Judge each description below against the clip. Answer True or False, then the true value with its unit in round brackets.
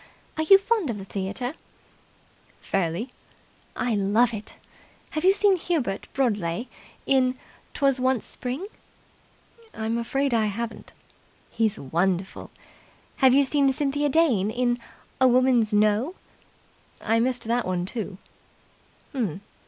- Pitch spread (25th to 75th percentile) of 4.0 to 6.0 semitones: True (4.7 semitones)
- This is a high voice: True (240 Hz)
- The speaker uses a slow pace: True (120 wpm)